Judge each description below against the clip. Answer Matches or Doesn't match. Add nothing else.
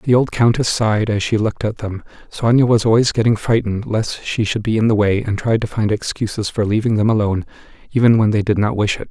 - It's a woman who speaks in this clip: Doesn't match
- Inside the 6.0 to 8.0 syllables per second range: Matches